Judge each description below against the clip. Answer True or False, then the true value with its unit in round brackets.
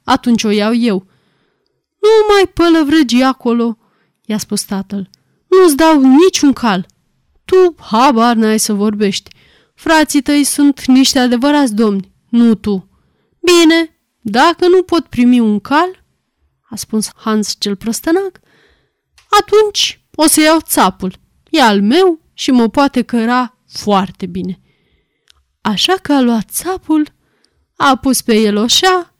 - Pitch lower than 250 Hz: False (255 Hz)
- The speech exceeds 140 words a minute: False (130 wpm)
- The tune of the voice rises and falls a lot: True (6.8 semitones)